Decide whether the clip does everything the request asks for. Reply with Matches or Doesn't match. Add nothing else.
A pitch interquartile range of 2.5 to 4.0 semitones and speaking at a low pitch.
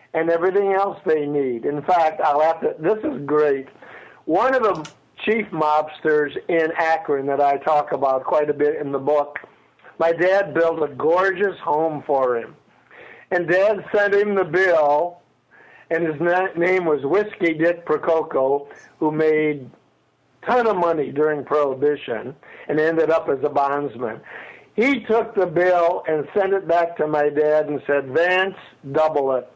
Doesn't match